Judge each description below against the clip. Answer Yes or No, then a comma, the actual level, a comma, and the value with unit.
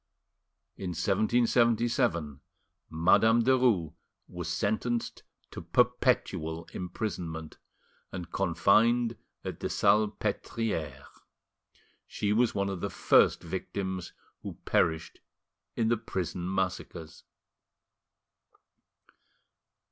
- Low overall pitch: Yes, very low, 95 Hz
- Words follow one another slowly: Yes, slow, 80 wpm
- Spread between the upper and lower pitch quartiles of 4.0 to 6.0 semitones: Yes, average, 5.0 semitones